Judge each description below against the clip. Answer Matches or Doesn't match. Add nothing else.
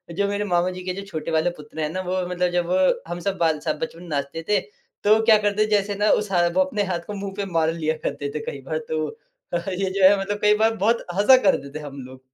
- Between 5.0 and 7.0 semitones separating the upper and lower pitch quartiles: Doesn't match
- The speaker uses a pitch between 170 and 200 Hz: Matches